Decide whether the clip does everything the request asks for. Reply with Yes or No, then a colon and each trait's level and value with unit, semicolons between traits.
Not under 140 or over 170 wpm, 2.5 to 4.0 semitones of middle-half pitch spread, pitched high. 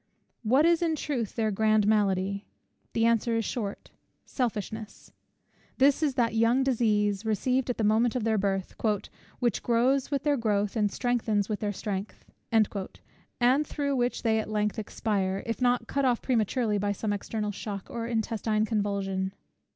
Yes: average, 160 wpm; average, 2.9 semitones; high, 220 Hz